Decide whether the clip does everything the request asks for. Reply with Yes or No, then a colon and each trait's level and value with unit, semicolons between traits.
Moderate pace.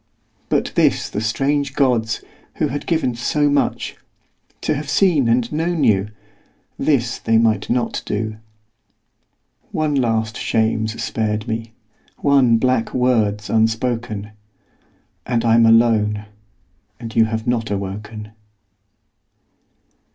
No: slow, 115 wpm